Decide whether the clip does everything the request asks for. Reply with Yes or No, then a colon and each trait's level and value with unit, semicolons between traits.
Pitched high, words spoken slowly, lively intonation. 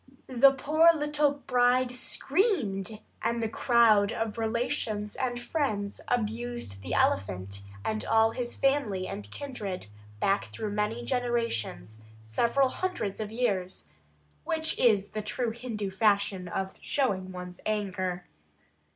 No: high, 220 Hz; slow, 125 wpm; average, 4.4 semitones